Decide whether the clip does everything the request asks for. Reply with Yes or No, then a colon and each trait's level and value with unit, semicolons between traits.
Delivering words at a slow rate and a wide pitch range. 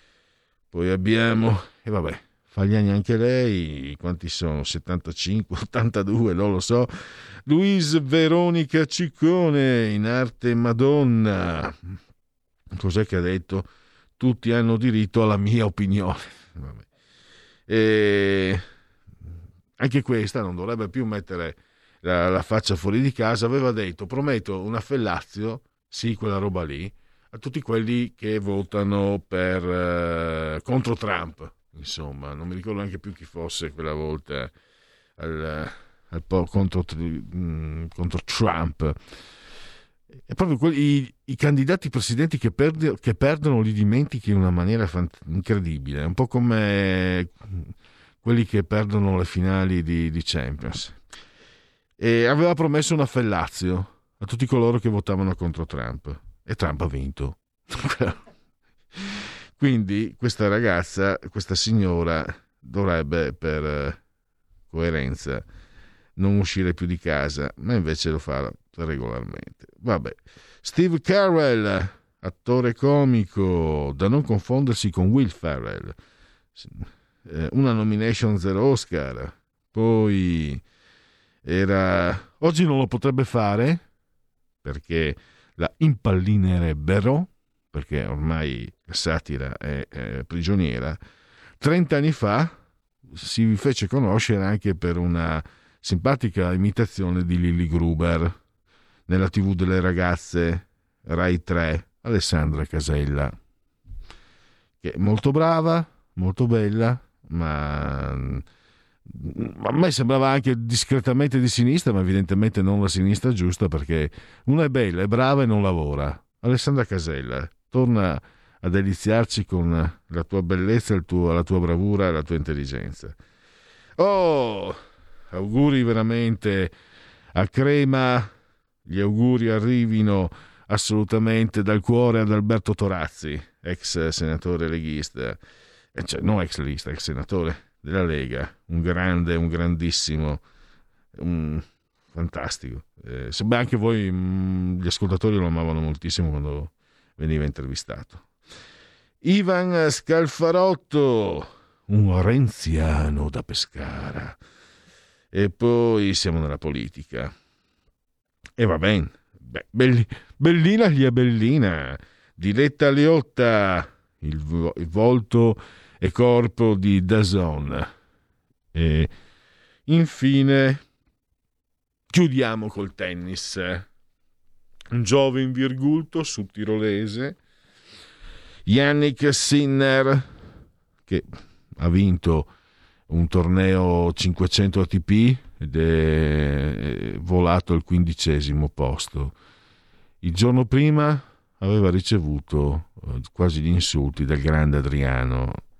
Yes: slow, 110 wpm; wide, 5.9 semitones